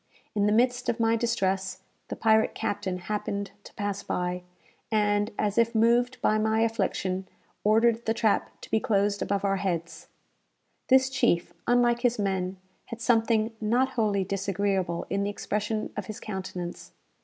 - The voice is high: Yes, high, 210 Hz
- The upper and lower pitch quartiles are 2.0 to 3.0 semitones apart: Yes, average, 2.7 semitones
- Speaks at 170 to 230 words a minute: No, average, 155 wpm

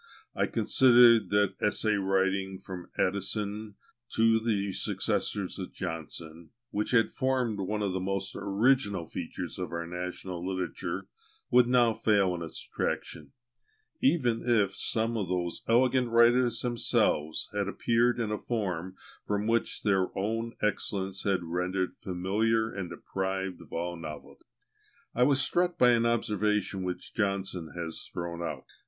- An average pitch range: Yes, average, 3.9 semitones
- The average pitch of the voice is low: Yes, low, 100 Hz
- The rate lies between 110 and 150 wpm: Yes, average, 140 wpm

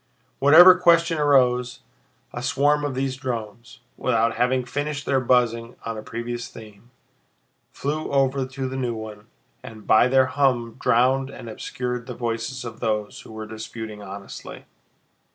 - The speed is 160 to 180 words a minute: No, average, 150 wpm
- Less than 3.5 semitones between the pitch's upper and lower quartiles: Yes, average, 2.9 semitones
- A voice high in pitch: No, low, 125 Hz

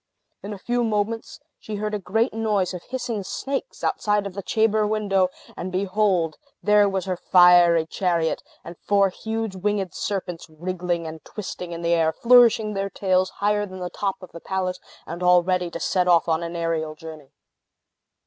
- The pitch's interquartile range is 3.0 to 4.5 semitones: Yes, average, 3.3 semitones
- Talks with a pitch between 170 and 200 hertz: Yes, medium, 185 Hz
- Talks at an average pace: Yes, average, 180 wpm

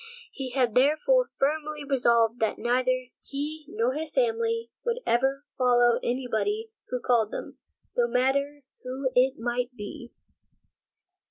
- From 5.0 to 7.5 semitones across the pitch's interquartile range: No, average, 3.9 semitones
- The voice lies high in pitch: Yes, very high, 265 Hz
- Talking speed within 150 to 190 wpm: No, slow, 135 wpm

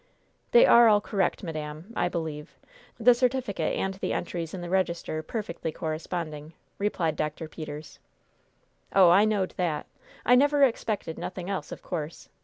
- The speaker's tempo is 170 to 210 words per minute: No, average, 150 wpm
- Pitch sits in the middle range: Yes, medium, 175 Hz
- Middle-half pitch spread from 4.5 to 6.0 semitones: Yes, average, 4.9 semitones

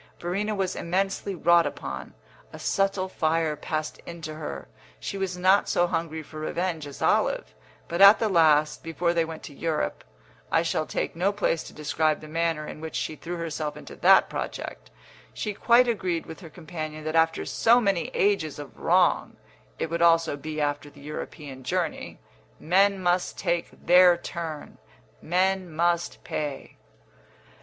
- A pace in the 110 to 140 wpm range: No, average, 165 wpm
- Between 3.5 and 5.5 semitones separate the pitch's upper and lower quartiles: No, average, 3.0 semitones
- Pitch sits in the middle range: Yes, medium, 165 Hz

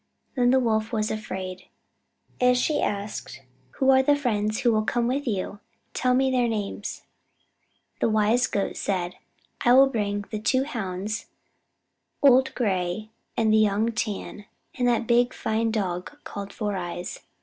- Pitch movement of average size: Yes, average, 3.5 semitones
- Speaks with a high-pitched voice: Yes, high, 220 Hz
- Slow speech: No, average, 150 wpm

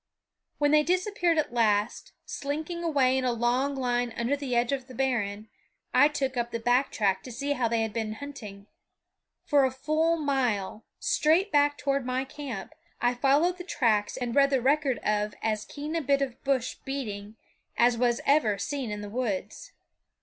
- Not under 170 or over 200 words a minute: Yes, average, 185 wpm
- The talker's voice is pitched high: Yes, very high, 260 Hz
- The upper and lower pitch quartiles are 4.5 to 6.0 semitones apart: No, average, 3.8 semitones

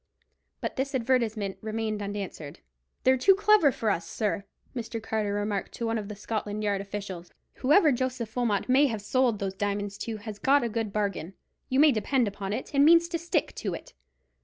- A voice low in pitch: No, high, 220 Hz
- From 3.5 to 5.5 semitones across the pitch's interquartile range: Yes, average, 4.2 semitones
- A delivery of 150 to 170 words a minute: No, average, 190 wpm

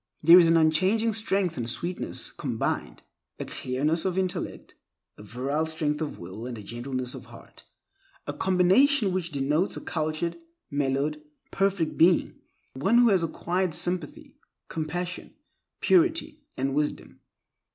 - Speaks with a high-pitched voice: No, medium, 165 Hz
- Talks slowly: Yes, slow, 130 wpm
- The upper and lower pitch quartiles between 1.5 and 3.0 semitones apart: No, average, 4.6 semitones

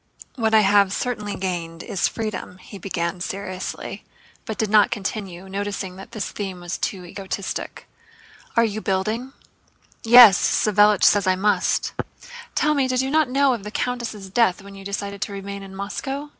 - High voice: Yes, high, 200 Hz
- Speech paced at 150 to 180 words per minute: Yes, average, 170 wpm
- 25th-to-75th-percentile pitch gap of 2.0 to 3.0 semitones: Yes, average, 2.7 semitones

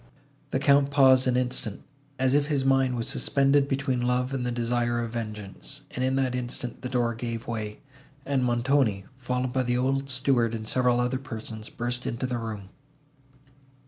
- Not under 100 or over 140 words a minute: No, average, 175 wpm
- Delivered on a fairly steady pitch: Yes, narrow, 2.1 semitones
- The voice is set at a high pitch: No, low, 125 Hz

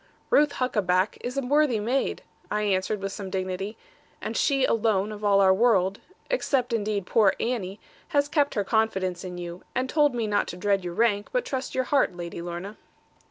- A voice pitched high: Yes, high, 210 Hz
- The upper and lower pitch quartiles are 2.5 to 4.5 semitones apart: No, average, 4.9 semitones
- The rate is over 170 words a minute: Yes, average, 190 wpm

